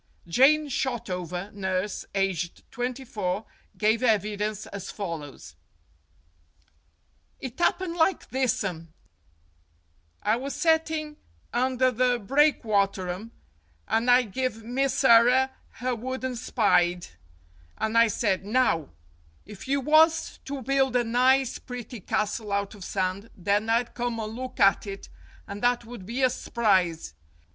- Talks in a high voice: Yes, high, 230 Hz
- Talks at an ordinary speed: No, slow, 125 wpm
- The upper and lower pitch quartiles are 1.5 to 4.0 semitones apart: No, average, 4.4 semitones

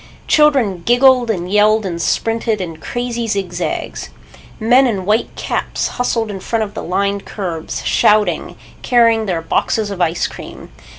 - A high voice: Yes, high, 215 Hz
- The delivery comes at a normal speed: Yes, average, 155 wpm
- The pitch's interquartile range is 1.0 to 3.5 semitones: No, average, 3.9 semitones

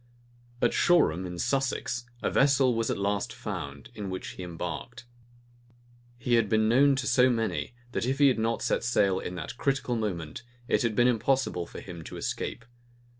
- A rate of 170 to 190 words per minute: Yes, average, 180 wpm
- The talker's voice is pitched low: Yes, low, 115 Hz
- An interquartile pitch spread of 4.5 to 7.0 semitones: Yes, average, 4.9 semitones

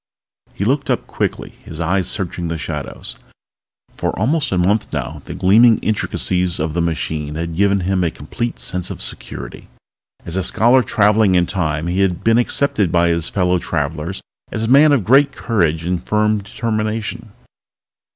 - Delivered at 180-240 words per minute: No, average, 170 wpm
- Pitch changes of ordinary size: Yes, average, 4.5 semitones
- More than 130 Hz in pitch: No, very low, 95 Hz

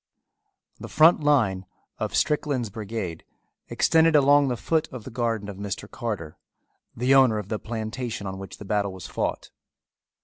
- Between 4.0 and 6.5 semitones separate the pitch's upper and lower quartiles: Yes, average, 5.0 semitones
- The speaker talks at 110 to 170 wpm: Yes, average, 160 wpm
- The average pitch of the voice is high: No, low, 115 Hz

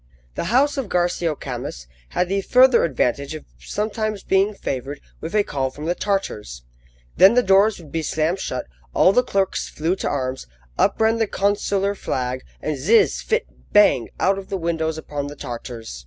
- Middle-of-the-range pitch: Yes, medium, 175 Hz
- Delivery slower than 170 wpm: No, average, 180 wpm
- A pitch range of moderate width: No, wide, 6.2 semitones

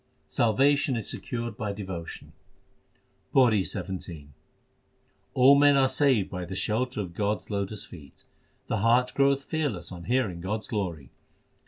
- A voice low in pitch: Yes, low, 110 Hz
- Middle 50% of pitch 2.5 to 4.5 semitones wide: No, wide, 5.6 semitones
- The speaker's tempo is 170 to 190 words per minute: No, average, 145 wpm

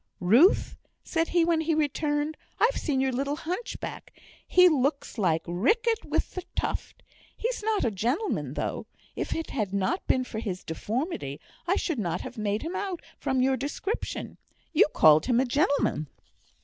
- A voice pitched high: Yes, very high, 280 Hz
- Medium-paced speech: Yes, average, 165 wpm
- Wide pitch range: Yes, wide, 7.7 semitones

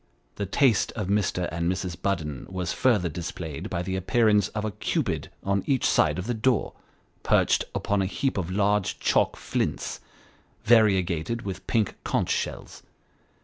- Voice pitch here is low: Yes, low, 100 Hz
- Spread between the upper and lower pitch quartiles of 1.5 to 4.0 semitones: Yes, average, 3.2 semitones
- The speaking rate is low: No, average, 155 wpm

